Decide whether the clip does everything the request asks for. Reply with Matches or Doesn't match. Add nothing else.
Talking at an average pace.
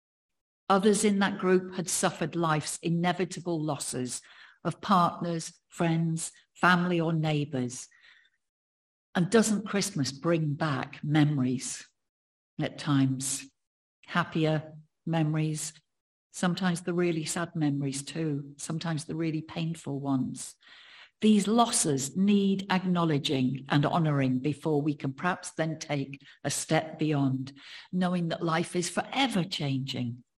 Doesn't match